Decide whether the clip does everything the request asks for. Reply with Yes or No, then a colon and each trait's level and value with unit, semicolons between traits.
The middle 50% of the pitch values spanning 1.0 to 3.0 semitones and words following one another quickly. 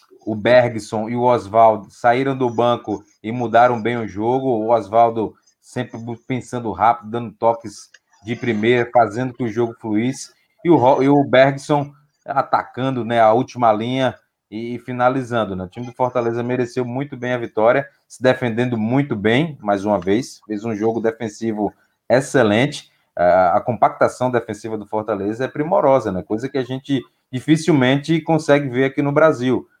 No: narrow, 2.6 semitones; average, 155 wpm